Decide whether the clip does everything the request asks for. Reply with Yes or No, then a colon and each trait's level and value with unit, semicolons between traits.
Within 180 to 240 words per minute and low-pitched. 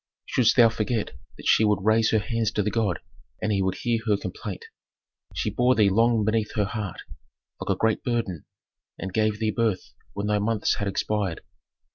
Yes: average, 190 wpm; low, 105 Hz